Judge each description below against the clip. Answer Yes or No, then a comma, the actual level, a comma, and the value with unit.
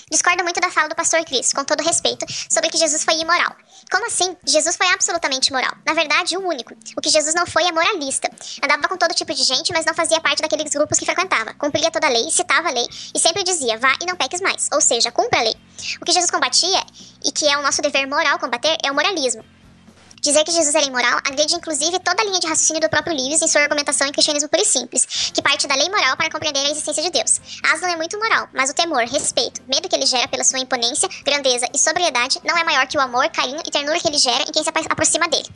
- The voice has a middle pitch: No, very high, 315 Hz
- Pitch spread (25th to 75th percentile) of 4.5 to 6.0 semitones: No, average, 2.9 semitones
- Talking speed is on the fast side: Yes, fast, 255 wpm